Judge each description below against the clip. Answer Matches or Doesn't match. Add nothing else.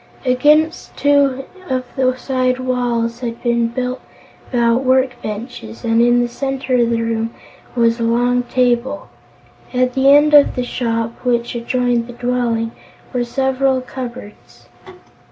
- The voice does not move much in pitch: Matches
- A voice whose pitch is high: Matches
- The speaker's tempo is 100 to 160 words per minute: Matches